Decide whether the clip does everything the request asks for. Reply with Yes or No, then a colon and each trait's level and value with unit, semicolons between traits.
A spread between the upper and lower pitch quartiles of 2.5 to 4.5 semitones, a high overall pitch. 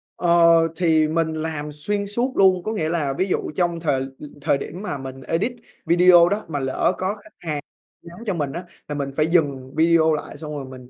No: average, 3.5 semitones; medium, 165 Hz